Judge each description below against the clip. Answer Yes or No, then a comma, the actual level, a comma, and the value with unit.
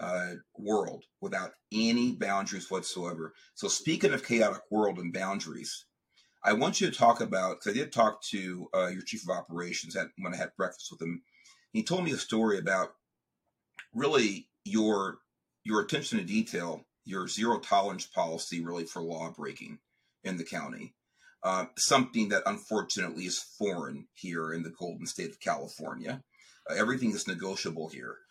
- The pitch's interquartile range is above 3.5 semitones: Yes, wide, 5.6 semitones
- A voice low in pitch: Yes, very low, 95 Hz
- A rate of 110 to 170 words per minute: Yes, average, 165 wpm